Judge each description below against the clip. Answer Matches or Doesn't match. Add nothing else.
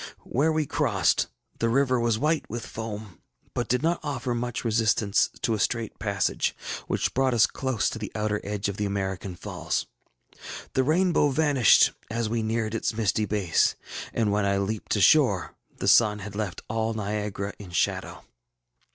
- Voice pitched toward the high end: Doesn't match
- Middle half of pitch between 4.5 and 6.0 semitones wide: Doesn't match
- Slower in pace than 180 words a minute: Matches